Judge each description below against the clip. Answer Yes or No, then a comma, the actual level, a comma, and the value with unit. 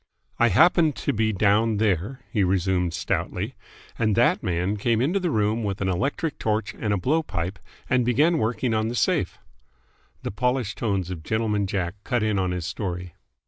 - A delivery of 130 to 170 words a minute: No, average, 185 wpm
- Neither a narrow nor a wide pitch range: Yes, average, 4.1 semitones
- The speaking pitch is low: Yes, low, 105 Hz